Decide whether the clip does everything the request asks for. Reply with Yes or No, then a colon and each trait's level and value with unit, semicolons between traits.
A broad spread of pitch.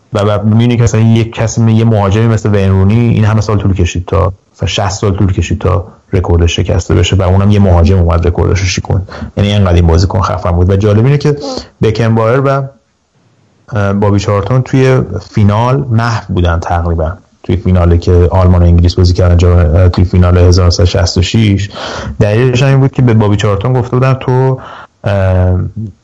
No: average, 3.6 semitones